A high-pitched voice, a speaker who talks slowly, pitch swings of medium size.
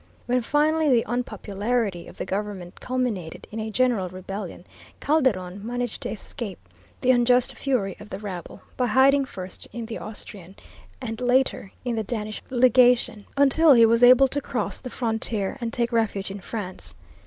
No: high, 230 Hz; average, 165 wpm; average, 3.9 semitones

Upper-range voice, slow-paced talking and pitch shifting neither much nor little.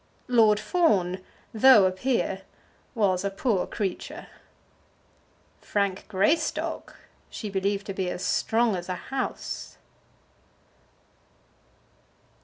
Yes: high, 200 Hz; slow, 95 wpm; average, 3.4 semitones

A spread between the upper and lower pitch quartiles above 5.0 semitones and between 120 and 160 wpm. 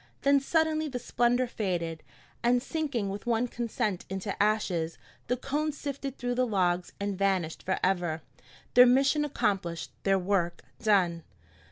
Yes: wide, 5.5 semitones; average, 140 wpm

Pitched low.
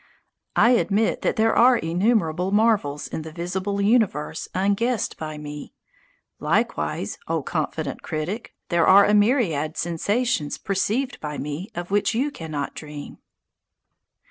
No: high, 190 Hz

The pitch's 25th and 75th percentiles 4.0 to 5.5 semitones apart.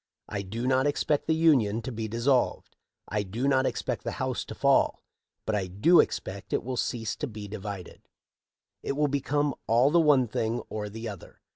Yes: average, 4.8 semitones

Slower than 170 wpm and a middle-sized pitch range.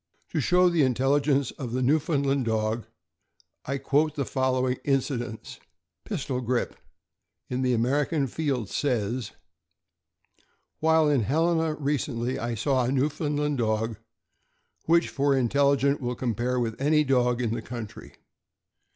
Yes: slow, 135 wpm; average, 3.1 semitones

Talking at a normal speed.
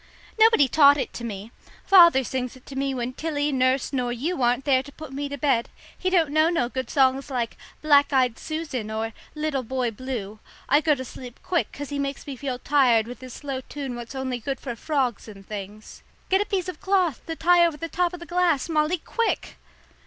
No: fast, 220 wpm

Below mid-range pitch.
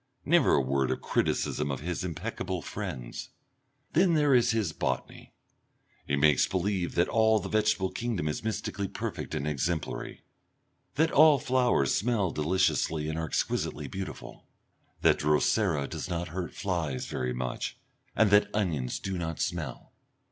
Yes: very low, 90 Hz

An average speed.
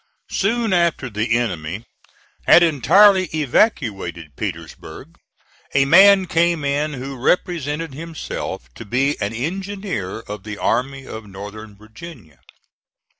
No: slow, 115 wpm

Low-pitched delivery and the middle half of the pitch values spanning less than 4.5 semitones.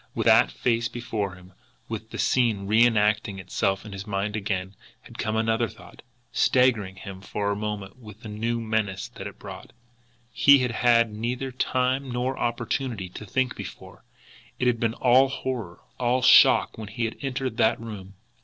Yes: low, 110 Hz; average, 3.3 semitones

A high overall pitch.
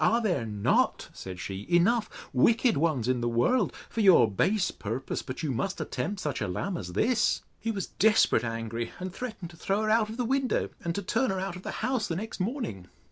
No: medium, 180 Hz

